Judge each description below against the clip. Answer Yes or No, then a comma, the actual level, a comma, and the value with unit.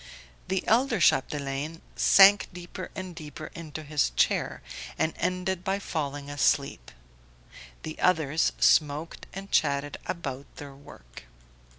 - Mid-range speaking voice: Yes, medium, 155 Hz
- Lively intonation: No, average, 4.3 semitones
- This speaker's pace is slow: Yes, slow, 115 wpm